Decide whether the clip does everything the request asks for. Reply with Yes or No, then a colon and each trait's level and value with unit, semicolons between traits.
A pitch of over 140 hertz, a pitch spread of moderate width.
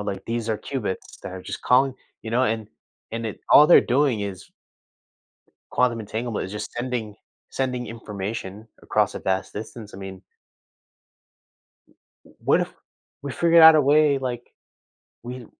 No: low, 115 Hz; average, 3.7 semitones